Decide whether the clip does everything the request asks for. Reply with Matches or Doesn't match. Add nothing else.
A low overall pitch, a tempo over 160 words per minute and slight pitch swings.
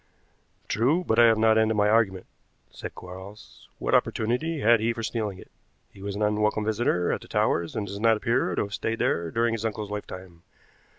Matches